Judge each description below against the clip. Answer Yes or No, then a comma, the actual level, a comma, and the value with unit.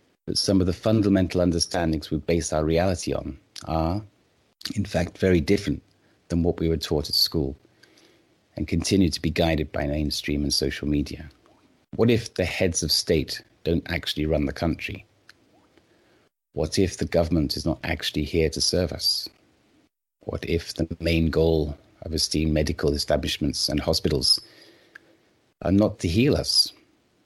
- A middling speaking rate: Yes, average, 155 wpm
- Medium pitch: No, very low, 85 Hz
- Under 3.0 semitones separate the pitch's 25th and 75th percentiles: No, average, 3.4 semitones